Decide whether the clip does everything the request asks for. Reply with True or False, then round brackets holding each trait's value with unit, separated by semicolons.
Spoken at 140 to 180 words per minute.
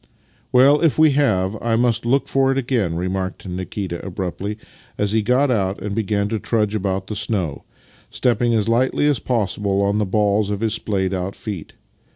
False (190 wpm)